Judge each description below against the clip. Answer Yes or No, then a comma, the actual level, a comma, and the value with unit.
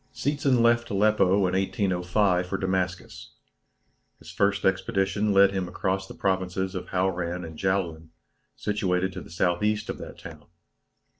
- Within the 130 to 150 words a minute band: Yes, average, 140 wpm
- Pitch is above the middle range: No, very low, 95 Hz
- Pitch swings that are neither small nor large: No, narrow, 2.1 semitones